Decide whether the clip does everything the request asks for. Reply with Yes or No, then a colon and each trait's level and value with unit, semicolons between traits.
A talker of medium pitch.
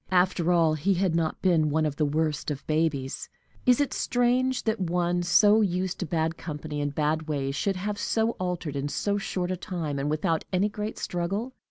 Yes: medium, 175 Hz